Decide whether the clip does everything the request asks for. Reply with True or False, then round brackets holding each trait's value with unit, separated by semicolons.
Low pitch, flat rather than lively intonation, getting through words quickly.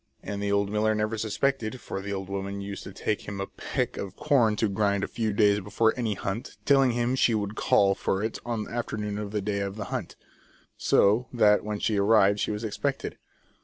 True (105 Hz; 1.8 semitones; 220 wpm)